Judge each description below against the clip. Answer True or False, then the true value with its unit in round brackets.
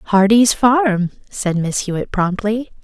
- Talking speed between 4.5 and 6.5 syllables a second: False (4.0 syllables/s)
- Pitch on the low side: False (210 Hz)